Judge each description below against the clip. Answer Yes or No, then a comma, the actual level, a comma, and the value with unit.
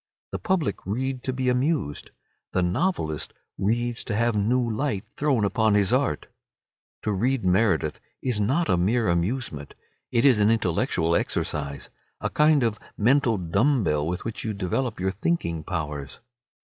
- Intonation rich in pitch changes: Yes, wide, 6.1 semitones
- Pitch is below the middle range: Yes, low, 110 Hz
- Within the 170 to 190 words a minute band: No, average, 155 wpm